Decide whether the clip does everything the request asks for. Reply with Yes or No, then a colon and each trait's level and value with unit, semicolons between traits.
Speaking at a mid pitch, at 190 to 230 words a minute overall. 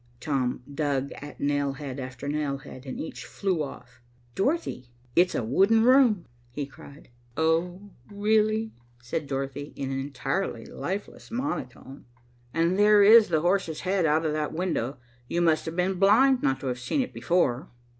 No: medium, 160 Hz; average, 165 wpm